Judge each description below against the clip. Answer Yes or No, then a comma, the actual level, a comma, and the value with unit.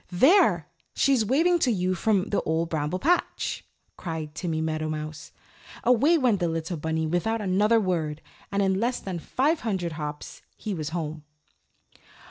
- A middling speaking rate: Yes, average, 150 wpm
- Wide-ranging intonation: Yes, wide, 6.0 semitones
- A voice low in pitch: No, medium, 185 Hz